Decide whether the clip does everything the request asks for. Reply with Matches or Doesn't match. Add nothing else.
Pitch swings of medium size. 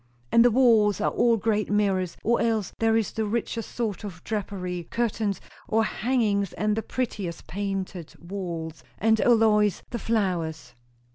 Matches